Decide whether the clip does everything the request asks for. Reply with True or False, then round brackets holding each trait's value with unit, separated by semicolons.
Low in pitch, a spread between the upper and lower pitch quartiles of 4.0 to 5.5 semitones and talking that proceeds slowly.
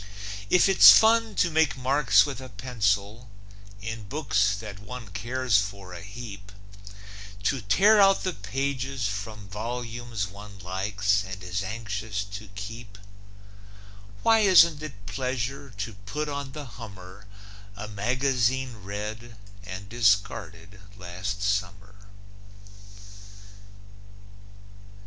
True (105 Hz; 4.4 semitones; 115 wpm)